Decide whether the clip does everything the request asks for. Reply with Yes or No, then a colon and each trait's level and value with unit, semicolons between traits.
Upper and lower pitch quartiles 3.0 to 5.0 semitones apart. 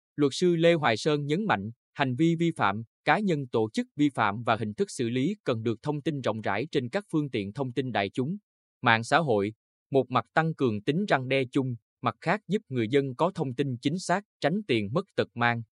No: wide, 5.5 semitones